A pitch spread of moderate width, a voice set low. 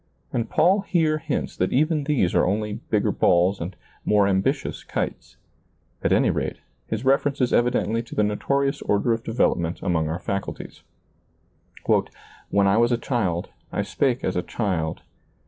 No: wide, 6.0 semitones; low, 115 Hz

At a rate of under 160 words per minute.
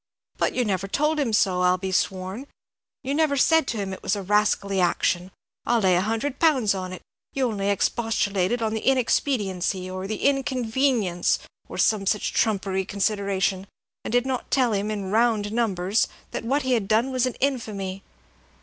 No: average, 180 wpm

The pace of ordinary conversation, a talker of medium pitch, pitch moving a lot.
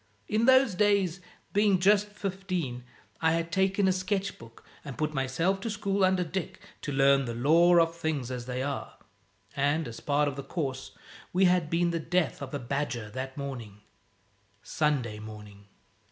Yes: average, 170 wpm; medium, 160 Hz; wide, 6.1 semitones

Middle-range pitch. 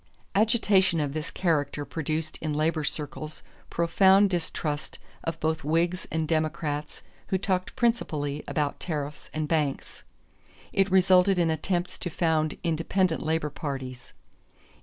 Yes: medium, 160 Hz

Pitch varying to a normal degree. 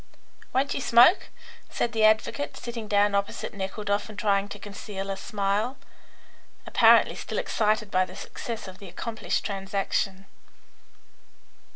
No: narrow, 1.9 semitones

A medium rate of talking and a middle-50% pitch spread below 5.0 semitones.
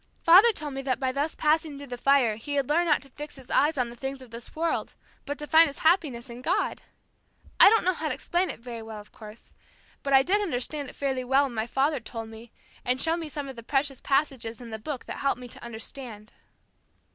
No: fast, 245 wpm; average, 4.0 semitones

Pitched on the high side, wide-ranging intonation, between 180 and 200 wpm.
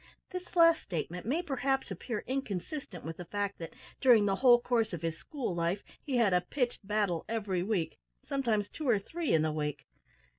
Yes: high, 210 Hz; wide, 6.9 semitones; average, 190 wpm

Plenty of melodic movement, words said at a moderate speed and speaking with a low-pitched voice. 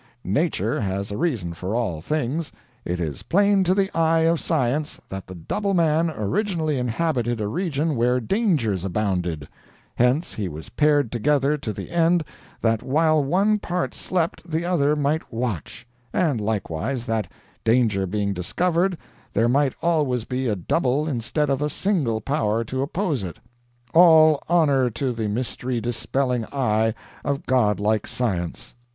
Yes: wide, 6.7 semitones; average, 150 wpm; low, 130 Hz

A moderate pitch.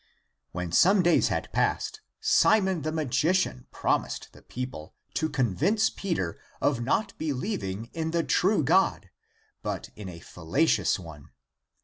Yes: medium, 150 Hz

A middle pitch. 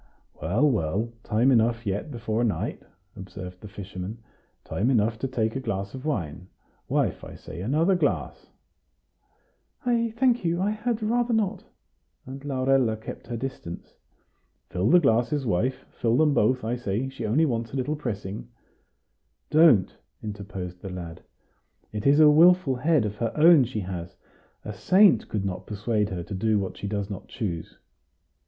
No: low, 115 Hz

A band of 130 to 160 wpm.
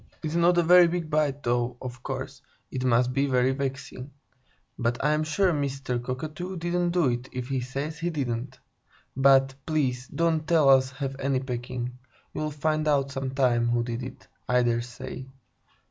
No: average, 170 wpm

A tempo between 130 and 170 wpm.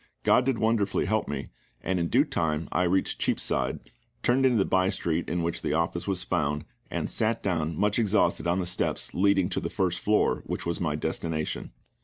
No: average, 200 wpm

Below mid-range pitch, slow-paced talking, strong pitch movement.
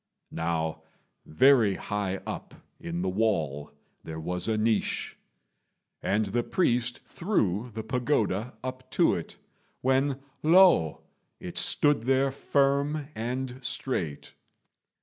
Yes: low, 115 Hz; slow, 110 wpm; wide, 6.3 semitones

